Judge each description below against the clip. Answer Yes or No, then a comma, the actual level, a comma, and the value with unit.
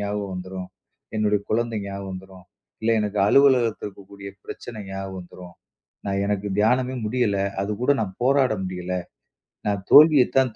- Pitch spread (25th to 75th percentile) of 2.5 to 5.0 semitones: Yes, average, 3.5 semitones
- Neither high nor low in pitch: No, low, 105 Hz